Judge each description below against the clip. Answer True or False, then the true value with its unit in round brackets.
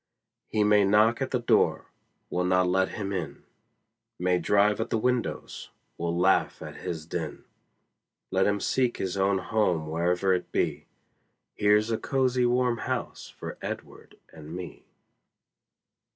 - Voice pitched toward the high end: False (100 Hz)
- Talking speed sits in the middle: True (145 wpm)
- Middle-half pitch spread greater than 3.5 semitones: True (3.9 semitones)